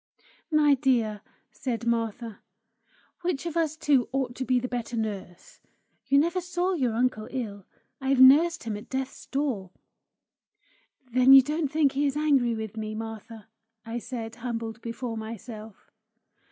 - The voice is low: No, very high, 250 Hz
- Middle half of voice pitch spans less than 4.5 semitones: Yes, average, 3.8 semitones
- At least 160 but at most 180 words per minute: No, average, 150 wpm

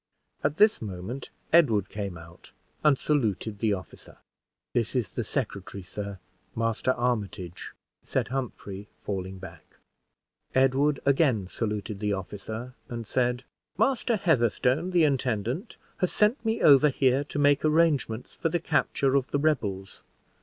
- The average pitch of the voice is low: Yes, low, 125 Hz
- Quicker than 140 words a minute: No, slow, 135 wpm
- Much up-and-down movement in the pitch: Yes, wide, 6.0 semitones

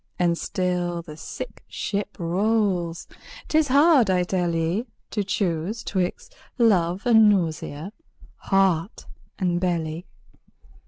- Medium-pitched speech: Yes, medium, 180 Hz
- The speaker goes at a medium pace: No, slow, 110 wpm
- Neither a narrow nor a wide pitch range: Yes, average, 3.5 semitones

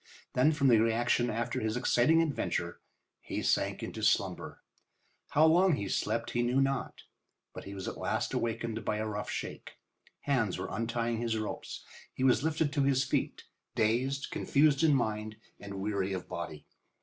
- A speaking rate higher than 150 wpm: Yes, average, 170 wpm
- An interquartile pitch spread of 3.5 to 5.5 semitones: Yes, average, 4.2 semitones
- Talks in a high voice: No, low, 120 Hz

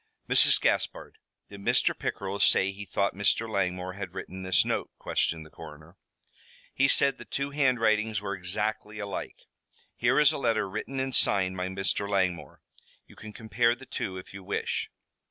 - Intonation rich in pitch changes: No, average, 3.3 semitones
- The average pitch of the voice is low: Yes, low, 100 Hz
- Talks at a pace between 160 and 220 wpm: Yes, average, 170 wpm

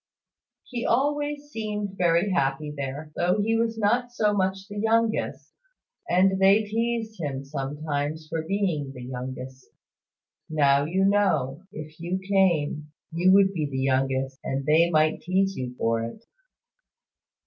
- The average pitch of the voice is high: No, medium, 170 Hz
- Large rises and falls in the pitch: Yes, wide, 6.4 semitones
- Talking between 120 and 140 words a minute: Yes, slow, 135 wpm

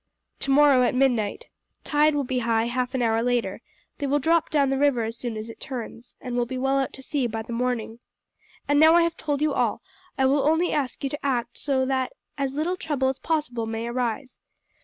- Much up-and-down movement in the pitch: No, average, 3.2 semitones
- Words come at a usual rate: No, fast, 225 wpm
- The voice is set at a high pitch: Yes, very high, 265 Hz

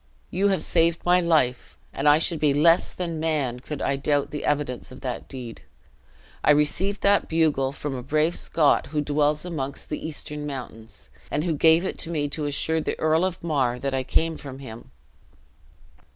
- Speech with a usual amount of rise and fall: Yes, average, 3.1 semitones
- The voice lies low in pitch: No, medium, 150 Hz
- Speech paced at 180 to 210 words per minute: Yes, average, 190 wpm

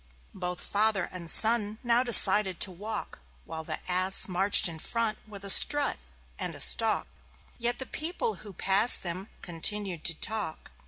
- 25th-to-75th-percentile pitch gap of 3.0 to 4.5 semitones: Yes, average, 3.7 semitones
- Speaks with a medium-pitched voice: No, high, 200 Hz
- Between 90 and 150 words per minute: No, average, 160 wpm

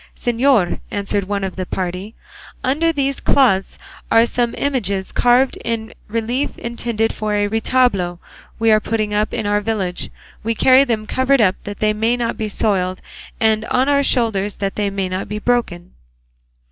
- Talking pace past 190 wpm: No, average, 170 wpm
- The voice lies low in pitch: No, high, 220 Hz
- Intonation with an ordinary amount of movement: Yes, average, 3.4 semitones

